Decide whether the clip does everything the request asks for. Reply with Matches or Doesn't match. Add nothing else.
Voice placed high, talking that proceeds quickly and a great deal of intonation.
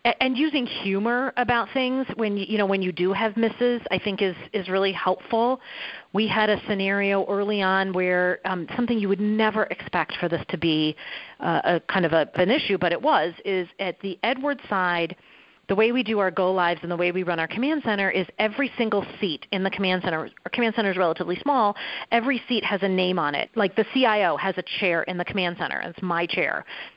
Doesn't match